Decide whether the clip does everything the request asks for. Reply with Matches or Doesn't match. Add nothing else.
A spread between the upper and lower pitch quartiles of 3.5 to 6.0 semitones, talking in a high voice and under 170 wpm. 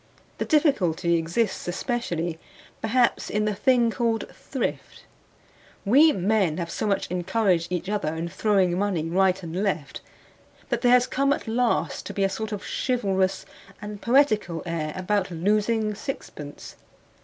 Matches